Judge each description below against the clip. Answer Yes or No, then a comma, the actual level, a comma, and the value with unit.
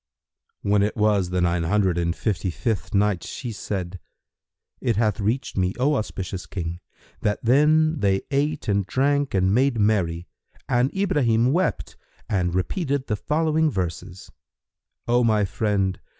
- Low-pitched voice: Yes, low, 105 Hz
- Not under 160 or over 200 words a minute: No, average, 145 wpm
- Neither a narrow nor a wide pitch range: No, wide, 6.0 semitones